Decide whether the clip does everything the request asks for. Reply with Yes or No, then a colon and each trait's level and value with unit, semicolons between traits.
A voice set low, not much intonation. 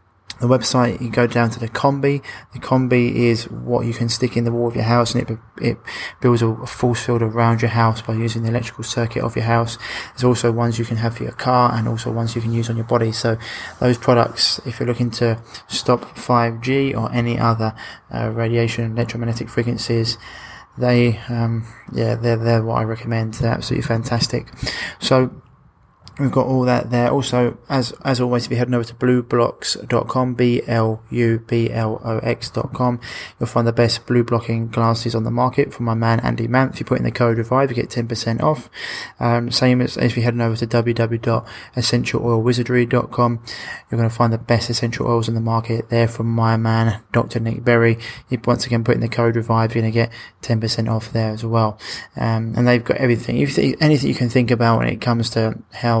Yes: low, 115 Hz; narrow, 1.1 semitones